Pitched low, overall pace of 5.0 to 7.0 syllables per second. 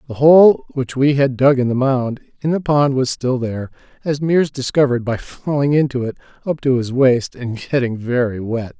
Yes: low, 130 Hz; 5.2 syllables/s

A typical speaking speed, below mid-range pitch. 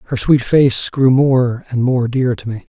No: fast, 220 wpm; low, 125 Hz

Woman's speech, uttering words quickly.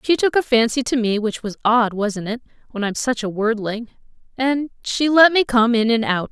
Yes: female; fast, 210 wpm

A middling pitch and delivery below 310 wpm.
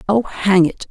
No: high, 195 Hz; average, 200 wpm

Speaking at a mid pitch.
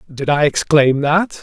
Yes: medium, 150 Hz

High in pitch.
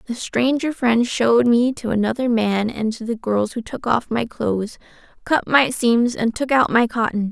Yes: high, 235 Hz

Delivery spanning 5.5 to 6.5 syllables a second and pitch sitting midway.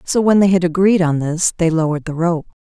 Yes: 6.0 syllables/s; medium, 170 Hz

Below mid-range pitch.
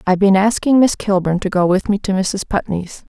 No: high, 195 Hz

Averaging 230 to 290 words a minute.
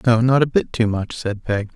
Yes: fast, 275 wpm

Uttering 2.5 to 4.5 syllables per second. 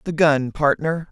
Yes: 4.0 syllables/s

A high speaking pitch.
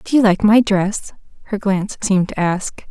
Yes: high, 200 Hz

